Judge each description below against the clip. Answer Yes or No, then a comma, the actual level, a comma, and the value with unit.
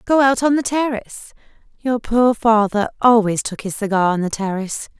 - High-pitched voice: Yes, high, 225 Hz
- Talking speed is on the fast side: No, average, 180 wpm